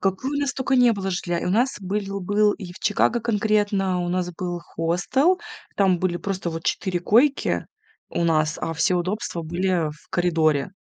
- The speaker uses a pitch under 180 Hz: No, medium, 185 Hz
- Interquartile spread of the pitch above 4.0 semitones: No, average, 3.4 semitones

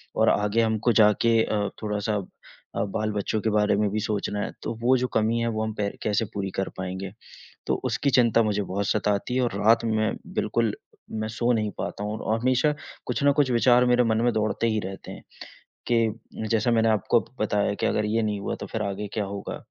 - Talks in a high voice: No, low, 110 Hz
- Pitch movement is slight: Yes, narrow, 2.0 semitones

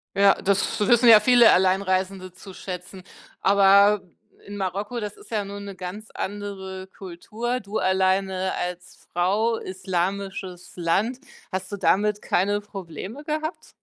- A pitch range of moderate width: No, narrow, 1.9 semitones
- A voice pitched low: No, high, 195 Hz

